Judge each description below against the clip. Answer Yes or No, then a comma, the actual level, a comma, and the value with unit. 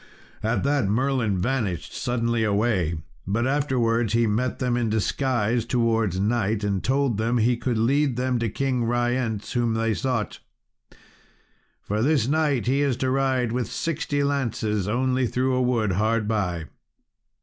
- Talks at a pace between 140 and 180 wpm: Yes, average, 150 wpm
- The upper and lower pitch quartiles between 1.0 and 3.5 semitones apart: Yes, average, 3.0 semitones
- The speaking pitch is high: No, low, 120 Hz